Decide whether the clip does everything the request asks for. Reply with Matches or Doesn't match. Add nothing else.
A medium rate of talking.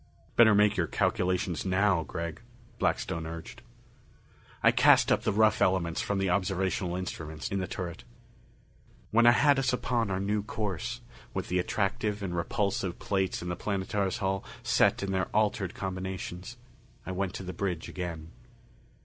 Matches